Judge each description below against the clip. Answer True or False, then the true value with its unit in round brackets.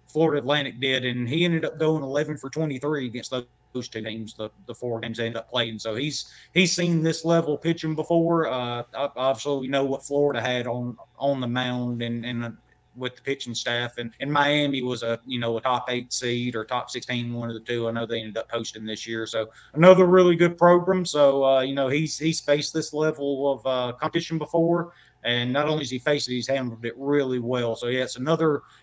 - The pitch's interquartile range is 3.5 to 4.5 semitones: True (3.9 semitones)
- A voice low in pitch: True (130 Hz)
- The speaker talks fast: True (230 wpm)